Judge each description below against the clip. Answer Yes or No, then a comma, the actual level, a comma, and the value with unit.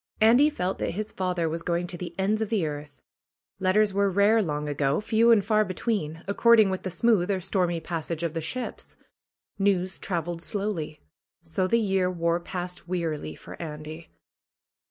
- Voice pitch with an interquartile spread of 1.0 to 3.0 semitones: No, average, 3.8 semitones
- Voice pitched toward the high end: No, medium, 180 Hz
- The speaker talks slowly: No, average, 175 wpm